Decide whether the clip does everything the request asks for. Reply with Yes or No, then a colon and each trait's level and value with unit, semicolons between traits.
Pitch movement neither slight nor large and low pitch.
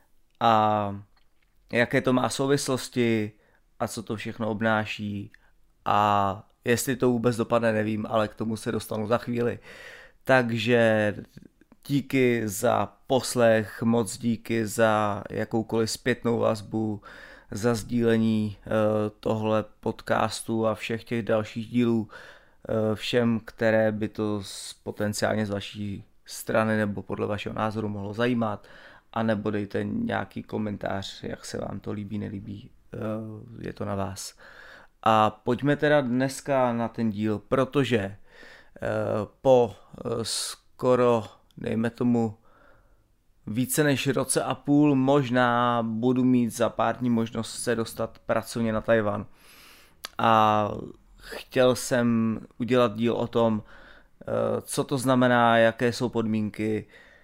No: narrow, 2.0 semitones; low, 115 Hz